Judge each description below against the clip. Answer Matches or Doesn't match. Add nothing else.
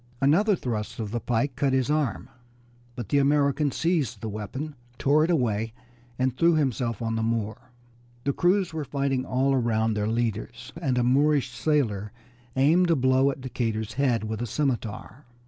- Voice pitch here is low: Matches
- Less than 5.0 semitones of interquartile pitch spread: Matches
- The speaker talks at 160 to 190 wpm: Matches